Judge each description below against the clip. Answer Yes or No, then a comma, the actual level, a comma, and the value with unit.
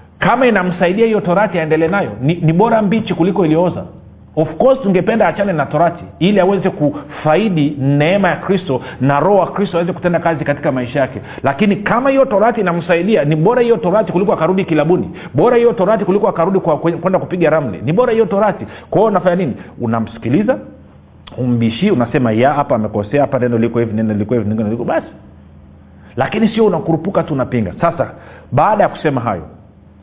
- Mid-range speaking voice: Yes, medium, 165 Hz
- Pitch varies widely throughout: Yes, wide, 7.2 semitones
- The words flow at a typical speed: No, fast, 155 wpm